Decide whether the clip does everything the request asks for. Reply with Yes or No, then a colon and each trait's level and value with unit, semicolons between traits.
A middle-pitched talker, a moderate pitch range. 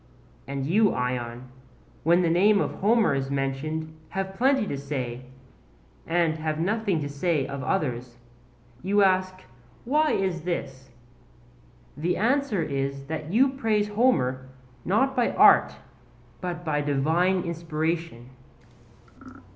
No: medium, 165 Hz; wide, 6.1 semitones